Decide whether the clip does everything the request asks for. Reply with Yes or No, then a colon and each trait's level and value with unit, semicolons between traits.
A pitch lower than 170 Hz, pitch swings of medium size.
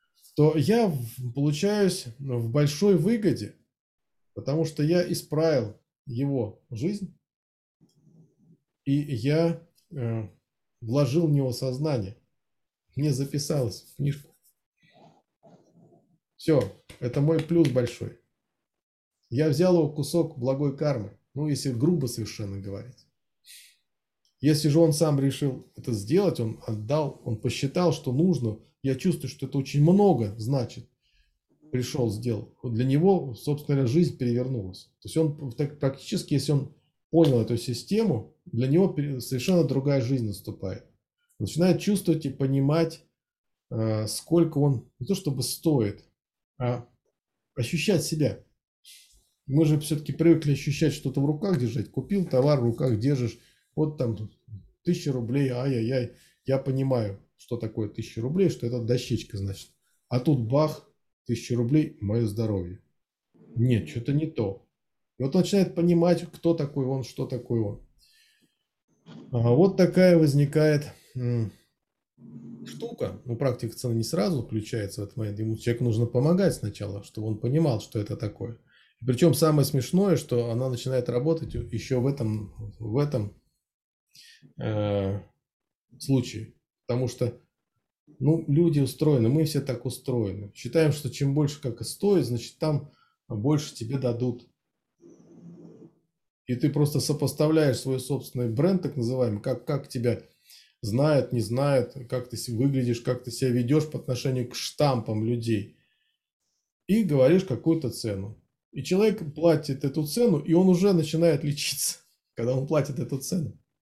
Yes: low, 135 Hz; average, 4.7 semitones